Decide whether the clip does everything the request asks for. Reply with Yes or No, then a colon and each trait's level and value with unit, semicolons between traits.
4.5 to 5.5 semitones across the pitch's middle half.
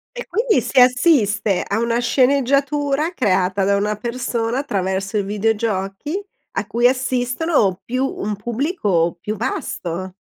Yes: average, 5.2 semitones